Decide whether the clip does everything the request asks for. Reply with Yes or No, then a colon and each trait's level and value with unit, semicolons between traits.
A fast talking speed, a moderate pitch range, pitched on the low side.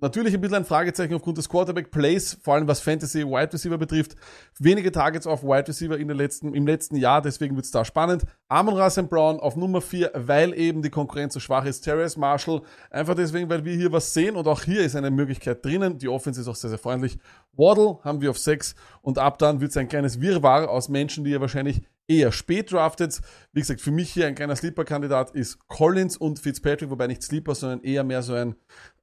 No: fast, 215 wpm; average, 3.3 semitones; medium, 150 Hz